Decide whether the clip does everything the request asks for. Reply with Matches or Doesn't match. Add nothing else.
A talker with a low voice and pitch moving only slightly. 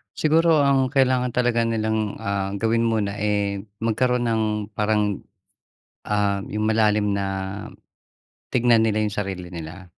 Doesn't match